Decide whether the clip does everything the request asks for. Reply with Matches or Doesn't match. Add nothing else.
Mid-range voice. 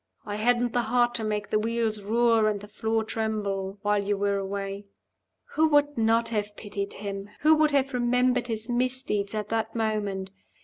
Doesn't match